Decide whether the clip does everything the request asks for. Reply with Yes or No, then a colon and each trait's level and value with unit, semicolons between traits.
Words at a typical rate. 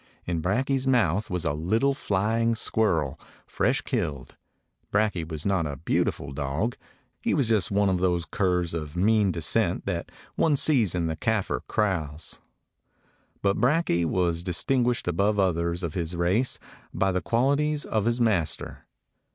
Yes: average, 150 wpm